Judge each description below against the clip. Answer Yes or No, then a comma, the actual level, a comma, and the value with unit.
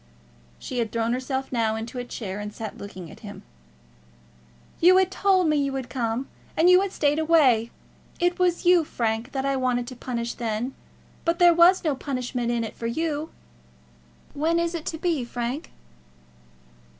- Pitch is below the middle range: No, very high, 265 Hz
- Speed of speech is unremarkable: Yes, average, 180 wpm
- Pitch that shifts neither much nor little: No, wide, 6.1 semitones